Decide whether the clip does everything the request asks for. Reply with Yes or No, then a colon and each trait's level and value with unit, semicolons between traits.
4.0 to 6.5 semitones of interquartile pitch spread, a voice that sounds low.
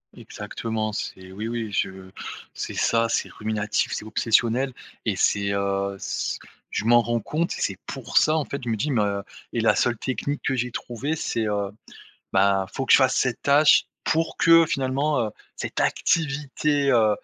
Yes: average, 5.0 semitones; low, 115 Hz